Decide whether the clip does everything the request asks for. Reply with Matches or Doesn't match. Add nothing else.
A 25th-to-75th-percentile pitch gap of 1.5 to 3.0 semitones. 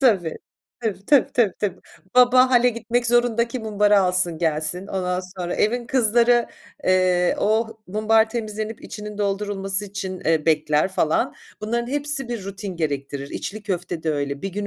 Doesn't match